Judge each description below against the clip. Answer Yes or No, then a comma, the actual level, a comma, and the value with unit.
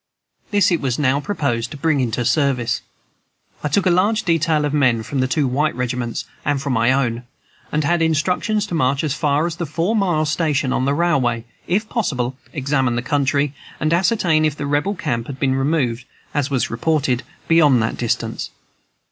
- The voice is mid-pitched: Yes, medium, 145 Hz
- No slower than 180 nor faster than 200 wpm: Yes, average, 190 wpm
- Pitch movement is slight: No, average, 4.2 semitones